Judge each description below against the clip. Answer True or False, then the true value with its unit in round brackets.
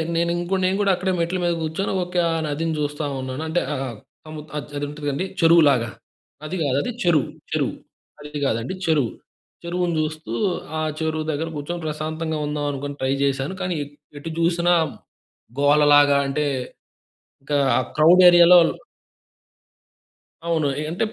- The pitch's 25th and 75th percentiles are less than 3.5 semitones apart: True (2.9 semitones)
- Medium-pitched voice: True (155 Hz)